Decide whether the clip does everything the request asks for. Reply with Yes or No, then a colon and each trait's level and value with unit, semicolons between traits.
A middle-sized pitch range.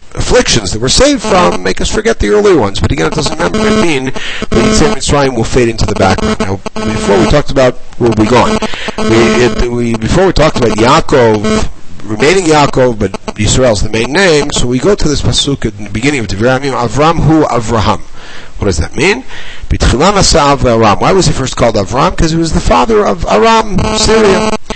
No: wide, 7.2 semitones